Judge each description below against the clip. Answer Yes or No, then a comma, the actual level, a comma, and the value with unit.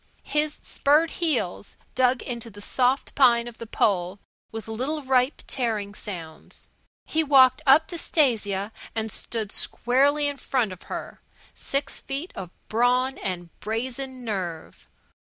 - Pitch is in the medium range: No, high, 245 Hz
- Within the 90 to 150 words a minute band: Yes, average, 140 wpm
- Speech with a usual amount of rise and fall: Yes, average, 4.7 semitones